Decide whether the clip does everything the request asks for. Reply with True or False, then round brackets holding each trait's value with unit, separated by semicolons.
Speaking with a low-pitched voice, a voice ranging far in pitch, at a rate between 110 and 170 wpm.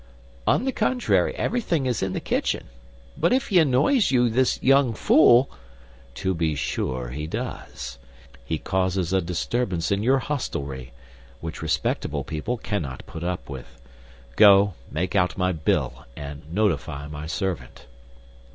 True (95 Hz; 8.3 semitones; 140 wpm)